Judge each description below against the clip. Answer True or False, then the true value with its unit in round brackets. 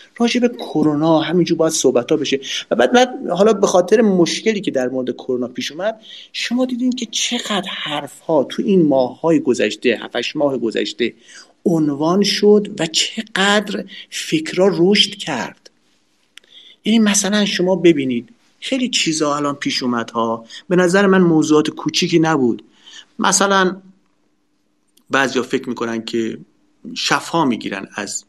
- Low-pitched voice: False (175 Hz)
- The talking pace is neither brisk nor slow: True (140 wpm)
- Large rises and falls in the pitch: True (6.1 semitones)